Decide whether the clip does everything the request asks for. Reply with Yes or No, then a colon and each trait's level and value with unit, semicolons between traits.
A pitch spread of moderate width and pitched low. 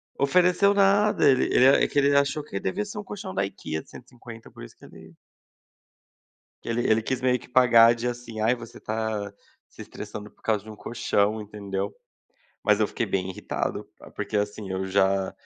Yes: average, 4.2 semitones; low, 110 Hz